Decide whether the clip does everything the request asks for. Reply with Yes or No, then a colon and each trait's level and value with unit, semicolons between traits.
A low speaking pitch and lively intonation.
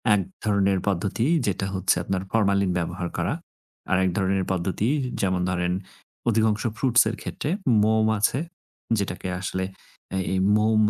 No: very low, 95 Hz; narrow, 2.5 semitones